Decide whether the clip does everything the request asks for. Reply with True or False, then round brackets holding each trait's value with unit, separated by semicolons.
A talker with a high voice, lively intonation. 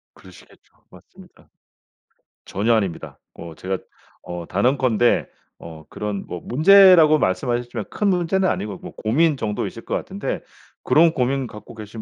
False (120 Hz; 7.4 semitones)